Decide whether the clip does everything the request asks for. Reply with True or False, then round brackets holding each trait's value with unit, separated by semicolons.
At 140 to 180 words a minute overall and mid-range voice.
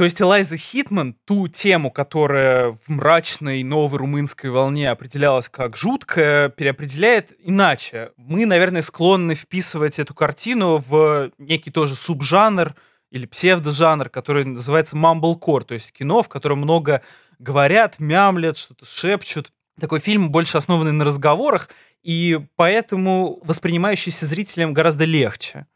False (125 wpm; 160 Hz)